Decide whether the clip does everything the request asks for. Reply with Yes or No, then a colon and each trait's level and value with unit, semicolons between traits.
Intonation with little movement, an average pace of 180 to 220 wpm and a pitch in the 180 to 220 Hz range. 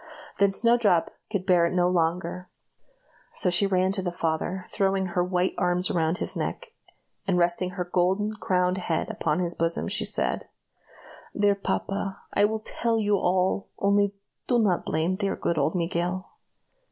No: narrow, 2.1 semitones; average, 165 wpm; medium, 185 Hz